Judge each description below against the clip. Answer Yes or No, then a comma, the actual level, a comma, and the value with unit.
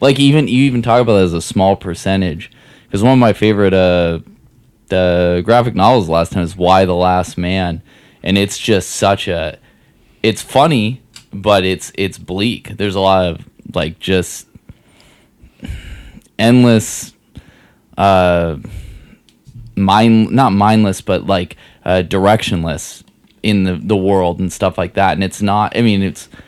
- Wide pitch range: No, average, 3.4 semitones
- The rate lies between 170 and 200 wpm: No, average, 155 wpm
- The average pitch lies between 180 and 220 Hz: No, very low, 95 Hz